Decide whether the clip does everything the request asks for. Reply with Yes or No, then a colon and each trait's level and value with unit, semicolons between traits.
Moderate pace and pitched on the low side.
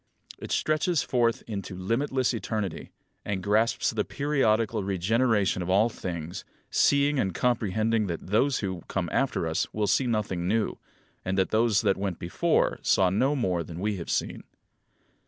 Yes: average, 155 wpm; low, 105 Hz